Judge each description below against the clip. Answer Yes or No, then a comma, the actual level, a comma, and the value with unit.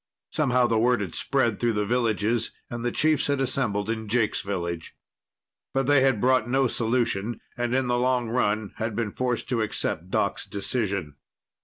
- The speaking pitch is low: Yes, low, 120 Hz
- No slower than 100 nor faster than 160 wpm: No, average, 175 wpm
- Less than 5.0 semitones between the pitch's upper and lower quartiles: Yes, average, 3.3 semitones